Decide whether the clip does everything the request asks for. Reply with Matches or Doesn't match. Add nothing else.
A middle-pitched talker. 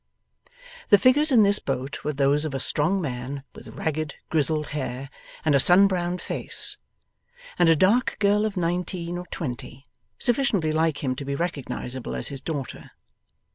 Matches